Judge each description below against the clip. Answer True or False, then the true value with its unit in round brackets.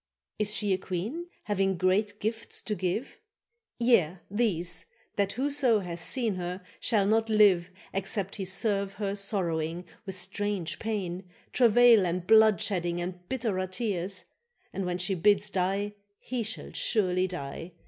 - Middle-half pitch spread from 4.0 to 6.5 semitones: False (3.1 semitones)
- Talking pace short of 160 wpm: True (140 wpm)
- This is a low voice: False (195 Hz)